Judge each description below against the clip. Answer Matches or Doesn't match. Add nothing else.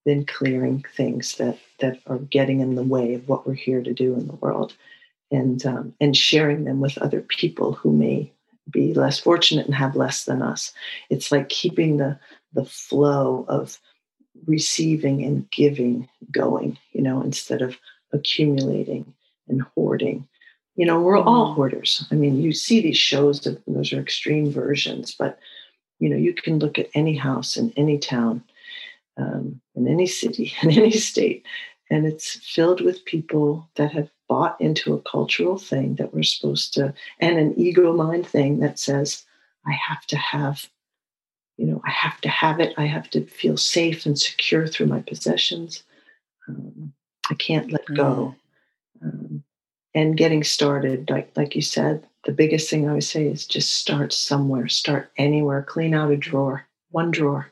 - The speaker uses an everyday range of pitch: Matches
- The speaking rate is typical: Matches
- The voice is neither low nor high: Matches